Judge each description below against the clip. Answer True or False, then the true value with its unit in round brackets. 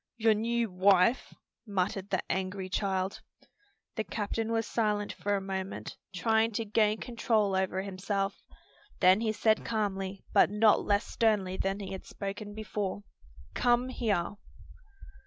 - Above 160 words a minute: False (140 wpm)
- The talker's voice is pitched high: True (205 Hz)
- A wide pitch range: False (2.4 semitones)